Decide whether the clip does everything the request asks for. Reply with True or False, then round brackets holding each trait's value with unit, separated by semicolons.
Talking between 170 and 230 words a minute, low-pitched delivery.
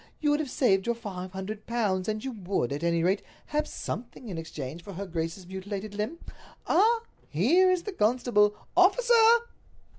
False (175 wpm; 210 Hz)